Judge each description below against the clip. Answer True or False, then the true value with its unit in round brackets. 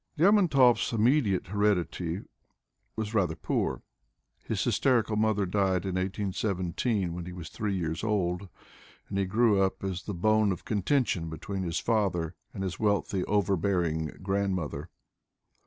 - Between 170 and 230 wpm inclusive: False (140 wpm)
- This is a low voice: True (95 Hz)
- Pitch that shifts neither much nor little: True (3.2 semitones)